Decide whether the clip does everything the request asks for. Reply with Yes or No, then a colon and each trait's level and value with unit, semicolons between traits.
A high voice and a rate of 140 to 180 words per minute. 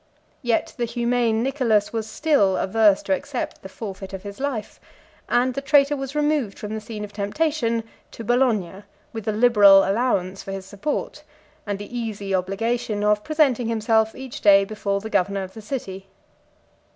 Yes: high, 220 Hz; average, 170 wpm